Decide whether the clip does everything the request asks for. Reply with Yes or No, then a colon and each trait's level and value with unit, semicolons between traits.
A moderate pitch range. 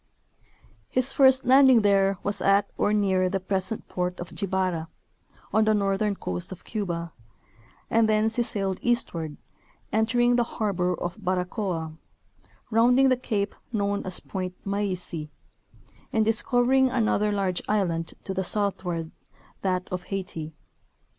Yes: average, 3.4 semitones